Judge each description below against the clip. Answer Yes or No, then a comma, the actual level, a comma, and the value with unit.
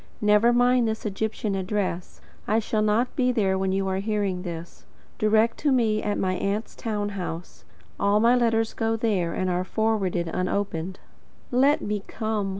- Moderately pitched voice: No, high, 210 Hz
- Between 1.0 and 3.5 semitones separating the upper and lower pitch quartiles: Yes, average, 2.8 semitones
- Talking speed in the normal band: Yes, average, 165 wpm